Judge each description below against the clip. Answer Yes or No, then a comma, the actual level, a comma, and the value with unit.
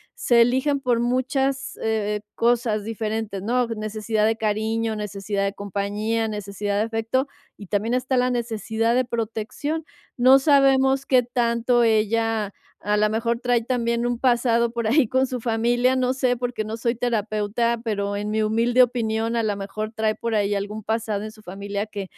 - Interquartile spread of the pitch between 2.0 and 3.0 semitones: Yes, narrow, 2.4 semitones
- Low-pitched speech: No, high, 225 Hz